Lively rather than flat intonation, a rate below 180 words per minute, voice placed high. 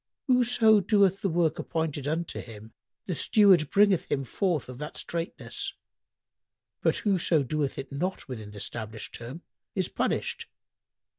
No: wide, 6.1 semitones; average, 140 wpm; medium, 160 Hz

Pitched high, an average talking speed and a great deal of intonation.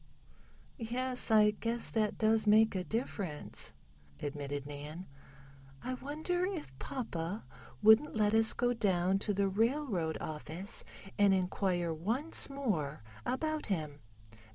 No: high, 210 Hz; slow, 120 wpm; wide, 5.9 semitones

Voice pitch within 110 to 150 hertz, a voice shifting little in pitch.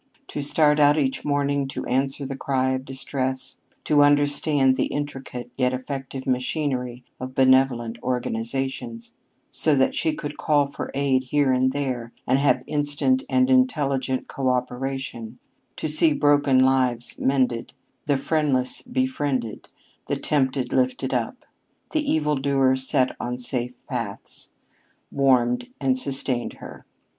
Yes: low, 135 Hz; narrow, 2.2 semitones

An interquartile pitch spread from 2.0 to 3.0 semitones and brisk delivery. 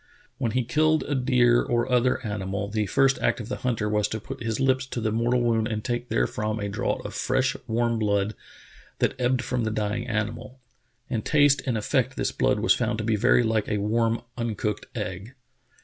Yes: average, 2.7 semitones; fast, 210 wpm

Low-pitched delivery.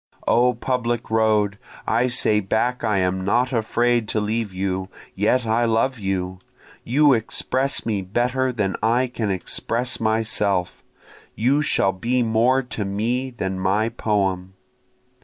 Yes: low, 110 Hz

